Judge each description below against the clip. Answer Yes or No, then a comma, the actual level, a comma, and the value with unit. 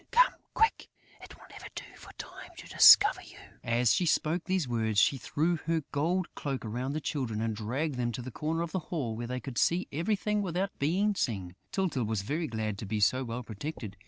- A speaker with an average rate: No, fast, 215 wpm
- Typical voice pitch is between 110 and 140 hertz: Yes, low, 135 Hz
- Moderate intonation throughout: No, wide, 7.0 semitones